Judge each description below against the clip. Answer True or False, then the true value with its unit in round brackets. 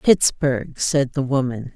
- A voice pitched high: False (135 Hz)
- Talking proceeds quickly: False (135 wpm)